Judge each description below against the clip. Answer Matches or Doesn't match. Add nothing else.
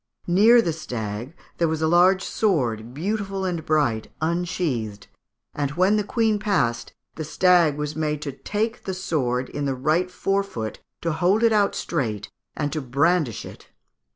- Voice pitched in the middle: Matches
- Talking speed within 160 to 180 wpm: Matches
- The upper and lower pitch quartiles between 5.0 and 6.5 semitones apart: Matches